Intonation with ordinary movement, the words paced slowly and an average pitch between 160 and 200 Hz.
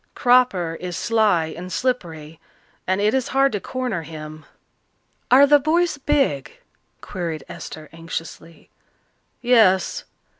No: wide, 7.6 semitones; slow, 115 wpm; high, 190 Hz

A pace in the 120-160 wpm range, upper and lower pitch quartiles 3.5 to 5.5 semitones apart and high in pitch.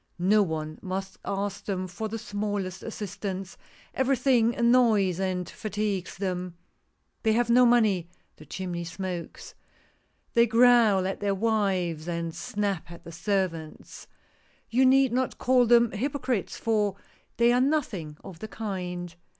Yes: average, 150 wpm; average, 4.4 semitones; high, 200 Hz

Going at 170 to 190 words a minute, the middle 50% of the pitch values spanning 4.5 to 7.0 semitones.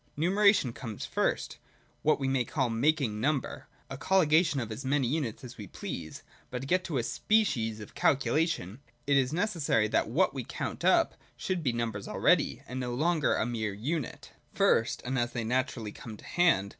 Yes: average, 180 wpm; average, 5.2 semitones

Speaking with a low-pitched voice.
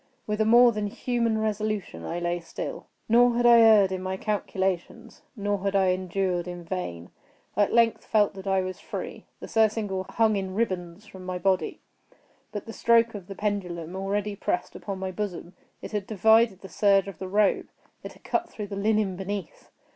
No: high, 200 Hz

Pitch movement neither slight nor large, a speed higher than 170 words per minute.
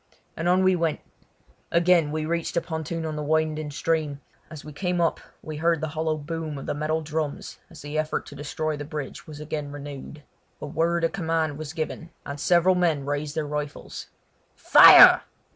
No: narrow, 1.9 semitones; average, 190 wpm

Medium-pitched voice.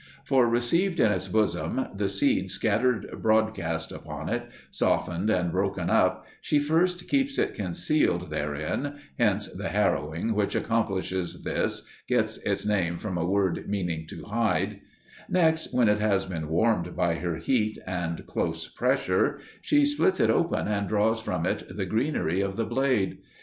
No: low, 105 Hz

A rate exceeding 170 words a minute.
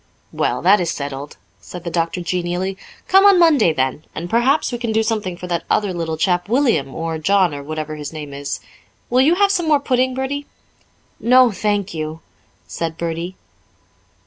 Yes: average, 180 wpm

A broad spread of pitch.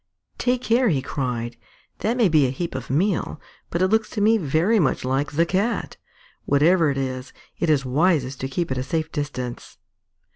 Yes: wide, 6.0 semitones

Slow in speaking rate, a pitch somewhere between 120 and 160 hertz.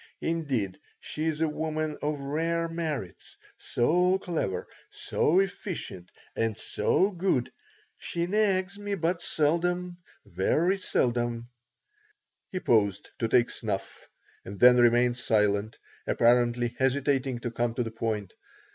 Yes: slow, 120 wpm; low, 135 Hz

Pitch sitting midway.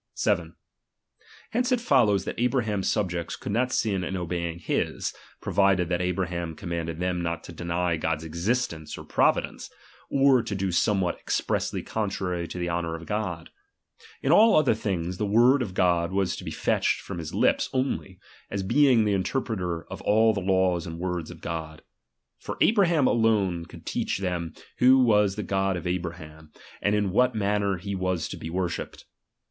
No: very low, 95 Hz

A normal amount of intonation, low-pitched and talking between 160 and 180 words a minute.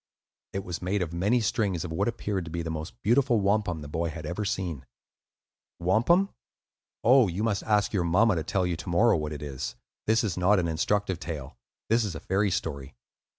No: average, 4.2 semitones; very low, 95 Hz; fast, 205 wpm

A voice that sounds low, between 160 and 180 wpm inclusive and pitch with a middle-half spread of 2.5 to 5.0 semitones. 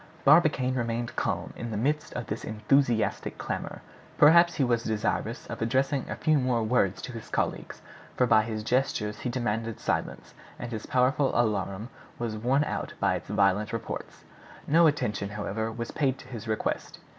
Yes: low, 120 Hz; average, 170 wpm; average, 3.5 semitones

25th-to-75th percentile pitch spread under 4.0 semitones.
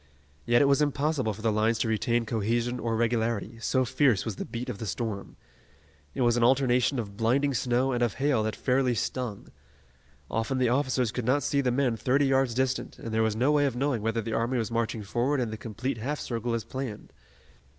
Yes: average, 2.7 semitones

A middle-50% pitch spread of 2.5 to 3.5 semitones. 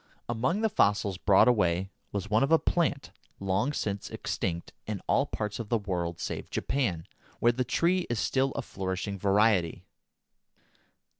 No: average, 5.0 semitones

